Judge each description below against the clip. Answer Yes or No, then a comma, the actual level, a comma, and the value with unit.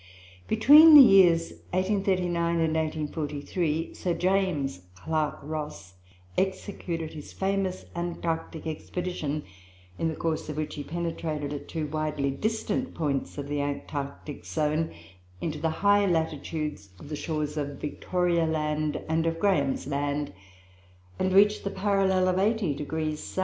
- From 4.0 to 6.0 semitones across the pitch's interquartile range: No, average, 3.6 semitones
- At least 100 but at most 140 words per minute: Yes, slow, 135 wpm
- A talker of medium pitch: Yes, medium, 160 Hz